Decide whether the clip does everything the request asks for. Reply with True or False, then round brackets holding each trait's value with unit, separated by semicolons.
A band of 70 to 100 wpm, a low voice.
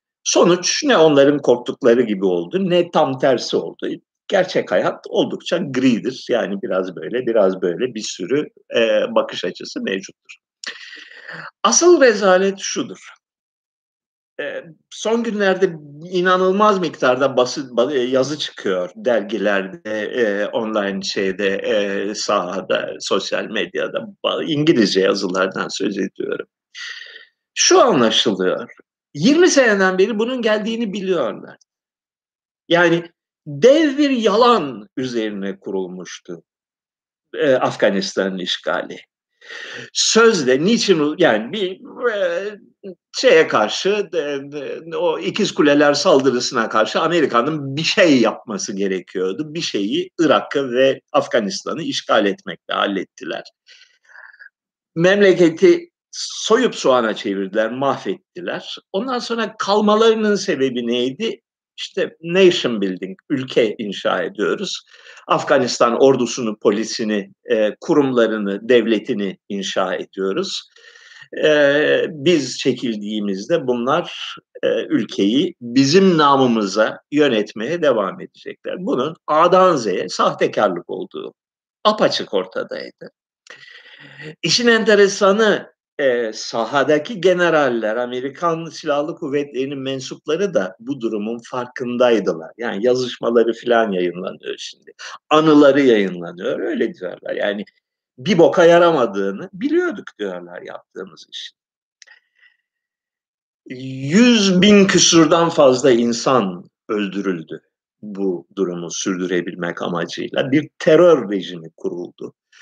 False (95 wpm; 170 Hz)